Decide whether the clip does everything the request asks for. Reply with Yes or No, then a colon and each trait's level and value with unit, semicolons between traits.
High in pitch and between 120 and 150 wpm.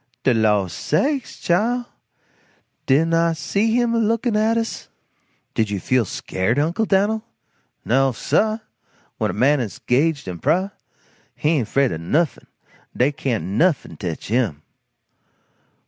No: medium, 150 Hz; average, 140 wpm